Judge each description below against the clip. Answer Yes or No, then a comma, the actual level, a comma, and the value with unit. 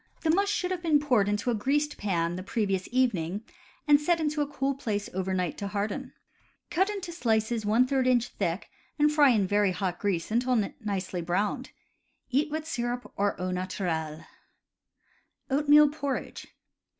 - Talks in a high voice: Yes, high, 235 Hz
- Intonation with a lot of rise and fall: Yes, wide, 7.0 semitones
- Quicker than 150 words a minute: Yes, average, 160 wpm